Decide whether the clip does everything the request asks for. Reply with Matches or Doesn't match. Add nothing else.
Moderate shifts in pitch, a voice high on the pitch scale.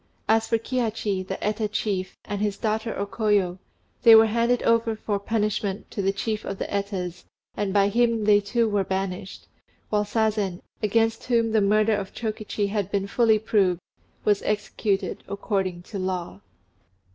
Doesn't match